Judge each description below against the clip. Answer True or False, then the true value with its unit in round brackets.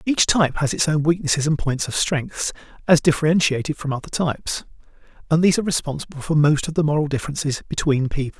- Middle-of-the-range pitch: True (155 Hz)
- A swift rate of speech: False (195 wpm)